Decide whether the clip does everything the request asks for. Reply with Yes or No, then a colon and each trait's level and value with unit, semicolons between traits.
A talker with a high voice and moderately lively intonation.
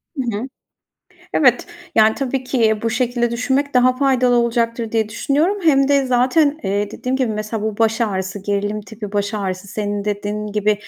Yes: high, 230 Hz; average, 3.5 semitones